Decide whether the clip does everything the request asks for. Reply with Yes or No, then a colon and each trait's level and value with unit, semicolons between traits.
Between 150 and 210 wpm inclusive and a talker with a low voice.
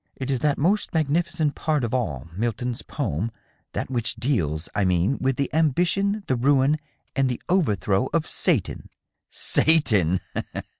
Yes: average, 160 wpm; low, 130 Hz